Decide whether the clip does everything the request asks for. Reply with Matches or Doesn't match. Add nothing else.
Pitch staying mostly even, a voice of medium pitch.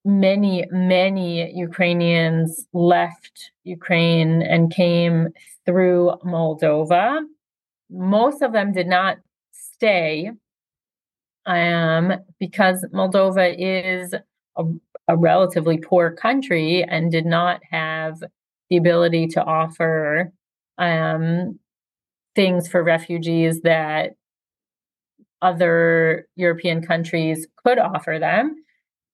Matches